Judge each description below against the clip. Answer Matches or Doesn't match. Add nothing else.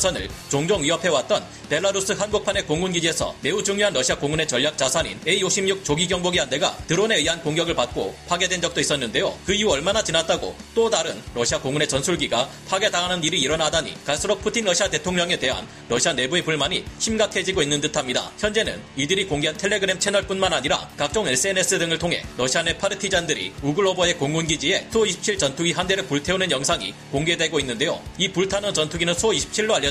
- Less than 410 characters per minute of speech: Doesn't match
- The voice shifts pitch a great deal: Doesn't match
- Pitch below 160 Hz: Doesn't match